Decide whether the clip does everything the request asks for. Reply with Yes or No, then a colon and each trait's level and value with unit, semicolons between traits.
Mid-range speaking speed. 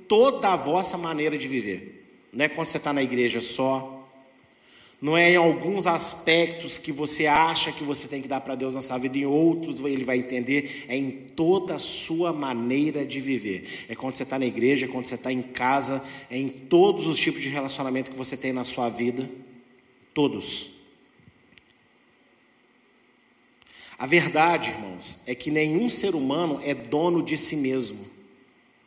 Yes: average, 175 wpm